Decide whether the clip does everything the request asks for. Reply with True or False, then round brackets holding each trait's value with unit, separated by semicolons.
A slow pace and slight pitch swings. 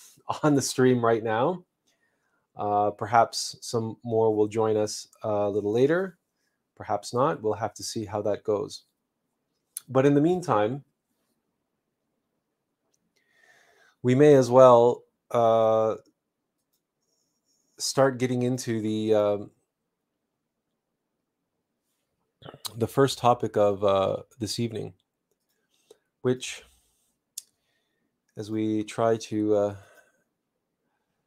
False (100 wpm; 3.2 semitones)